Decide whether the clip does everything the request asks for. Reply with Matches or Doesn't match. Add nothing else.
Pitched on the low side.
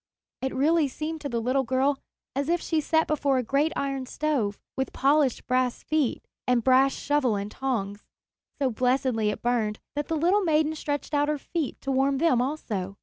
Doesn't match